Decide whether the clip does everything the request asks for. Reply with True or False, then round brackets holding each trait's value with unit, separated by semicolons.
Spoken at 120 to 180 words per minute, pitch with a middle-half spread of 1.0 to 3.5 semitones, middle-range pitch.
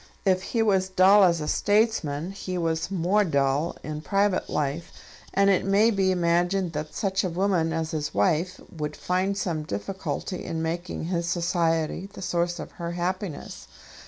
True (165 wpm; 3.0 semitones; 175 Hz)